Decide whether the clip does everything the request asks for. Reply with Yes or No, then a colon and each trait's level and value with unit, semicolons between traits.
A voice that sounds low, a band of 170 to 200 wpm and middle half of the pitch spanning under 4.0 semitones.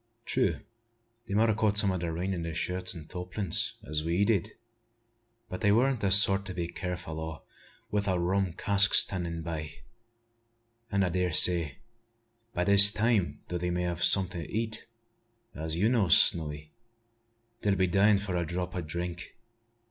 Yes: very low, 90 Hz; average, 180 wpm; average, 2.9 semitones